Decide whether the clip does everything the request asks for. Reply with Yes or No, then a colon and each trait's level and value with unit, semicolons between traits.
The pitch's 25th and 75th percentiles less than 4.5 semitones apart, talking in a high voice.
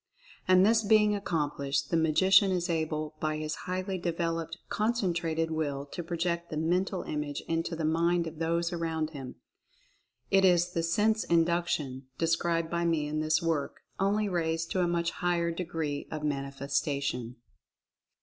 No: narrow, 2.4 semitones; medium, 165 Hz